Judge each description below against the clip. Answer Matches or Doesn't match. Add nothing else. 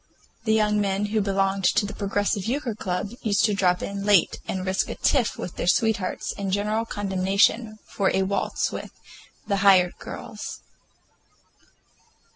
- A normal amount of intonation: Doesn't match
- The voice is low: Doesn't match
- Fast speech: Doesn't match